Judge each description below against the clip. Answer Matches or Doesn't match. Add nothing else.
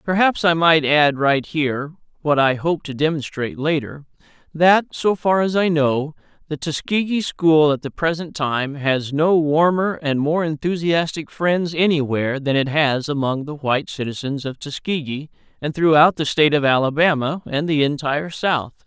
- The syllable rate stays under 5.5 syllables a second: Matches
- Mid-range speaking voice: Matches